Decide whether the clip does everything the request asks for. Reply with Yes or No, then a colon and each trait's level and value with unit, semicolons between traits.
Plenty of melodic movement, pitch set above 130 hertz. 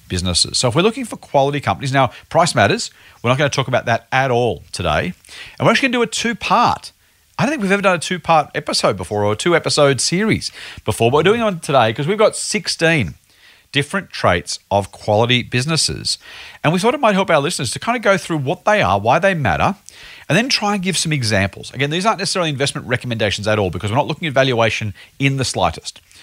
Yes: wide, 8.4 semitones; medium, 140 Hz